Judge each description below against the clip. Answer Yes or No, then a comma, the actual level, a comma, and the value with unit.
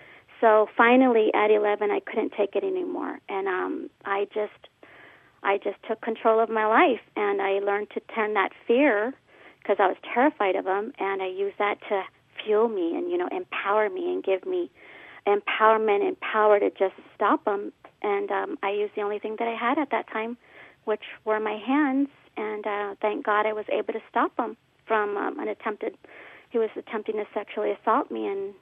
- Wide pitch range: Yes, wide, 6.4 semitones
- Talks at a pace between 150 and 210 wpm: Yes, average, 195 wpm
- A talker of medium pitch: No, high, 220 Hz